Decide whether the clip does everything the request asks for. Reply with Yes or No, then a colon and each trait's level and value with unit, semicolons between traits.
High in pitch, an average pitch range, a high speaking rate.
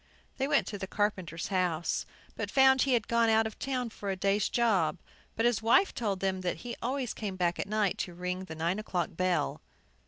Yes: high, 205 Hz; average, 4.2 semitones; fast, 215 wpm